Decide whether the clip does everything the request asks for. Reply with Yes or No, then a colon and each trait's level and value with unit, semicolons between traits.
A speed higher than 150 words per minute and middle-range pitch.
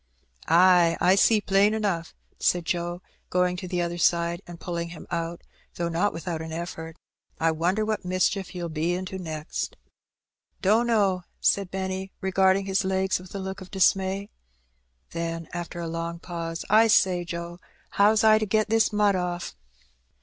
Yes: average, 165 wpm; medium, 180 Hz